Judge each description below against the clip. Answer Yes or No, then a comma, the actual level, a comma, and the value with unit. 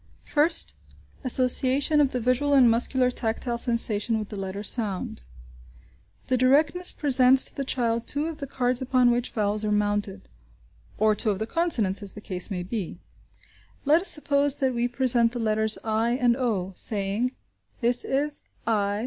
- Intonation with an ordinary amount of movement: Yes, average, 3.6 semitones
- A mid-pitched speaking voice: No, high, 240 Hz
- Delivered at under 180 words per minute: Yes, average, 165 wpm